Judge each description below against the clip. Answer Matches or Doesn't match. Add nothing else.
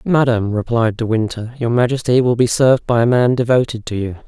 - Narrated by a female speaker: Doesn't match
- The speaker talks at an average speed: Doesn't match